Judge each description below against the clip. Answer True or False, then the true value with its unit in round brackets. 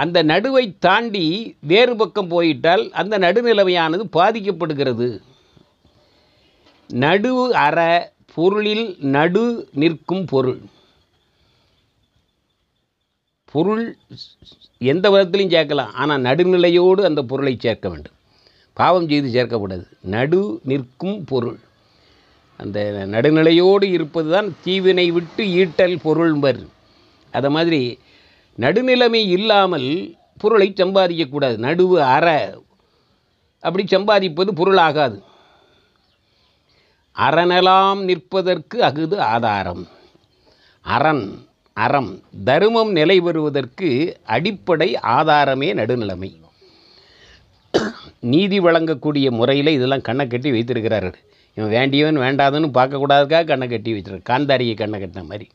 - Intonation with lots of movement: True (6.9 semitones)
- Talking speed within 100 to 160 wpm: False (85 wpm)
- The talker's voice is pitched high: False (155 Hz)